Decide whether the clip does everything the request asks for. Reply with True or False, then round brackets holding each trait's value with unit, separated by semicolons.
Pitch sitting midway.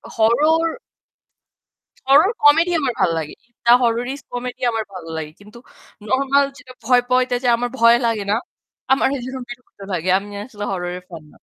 False (245 Hz)